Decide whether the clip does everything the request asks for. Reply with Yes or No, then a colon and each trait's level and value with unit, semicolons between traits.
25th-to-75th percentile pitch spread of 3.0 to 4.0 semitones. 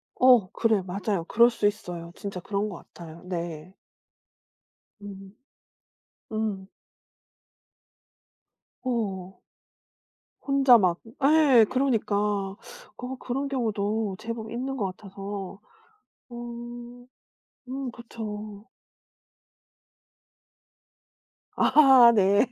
Yes: average, 3.7 semitones